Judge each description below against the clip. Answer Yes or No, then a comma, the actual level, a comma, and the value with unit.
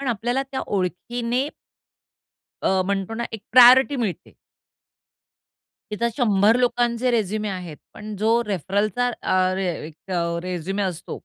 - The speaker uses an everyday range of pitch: Yes, average, 4.1 semitones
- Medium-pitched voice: No, high, 215 Hz